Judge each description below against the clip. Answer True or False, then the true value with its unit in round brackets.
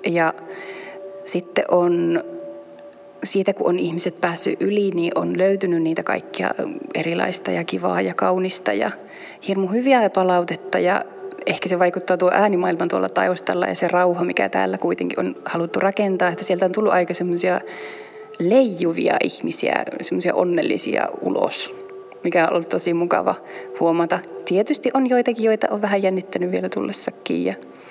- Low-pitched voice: False (185 Hz)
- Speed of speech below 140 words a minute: False (145 wpm)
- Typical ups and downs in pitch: True (3.2 semitones)